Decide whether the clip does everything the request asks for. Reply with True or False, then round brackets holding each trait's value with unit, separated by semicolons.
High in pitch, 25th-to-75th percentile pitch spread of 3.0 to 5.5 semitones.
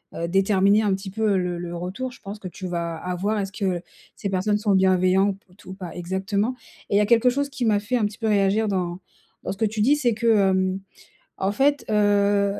False (200 Hz; 2.4 semitones)